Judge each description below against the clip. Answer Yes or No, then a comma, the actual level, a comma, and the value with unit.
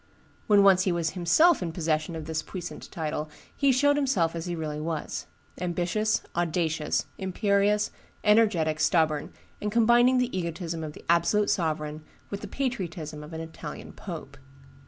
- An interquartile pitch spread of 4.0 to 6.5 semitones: Yes, average, 4.6 semitones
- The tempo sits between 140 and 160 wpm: Yes, average, 155 wpm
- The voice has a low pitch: No, medium, 170 Hz